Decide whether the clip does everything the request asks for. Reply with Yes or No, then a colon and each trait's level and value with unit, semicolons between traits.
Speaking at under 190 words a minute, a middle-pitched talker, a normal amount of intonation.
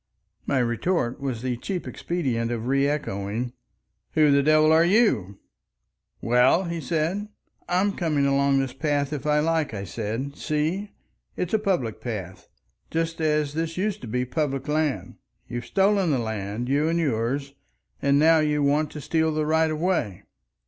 Yes: average, 160 wpm; medium, 145 Hz; average, 4.7 semitones